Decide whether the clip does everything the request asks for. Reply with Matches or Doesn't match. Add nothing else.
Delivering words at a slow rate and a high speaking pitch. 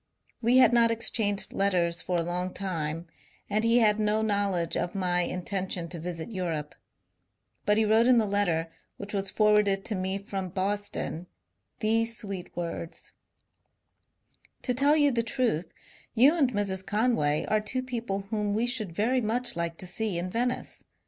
Doesn't match